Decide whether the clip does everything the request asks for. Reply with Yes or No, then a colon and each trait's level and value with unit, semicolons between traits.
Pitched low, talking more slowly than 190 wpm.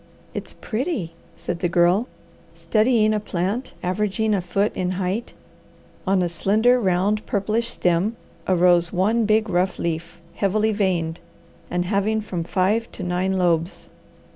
No: high, 190 Hz; average, 140 wpm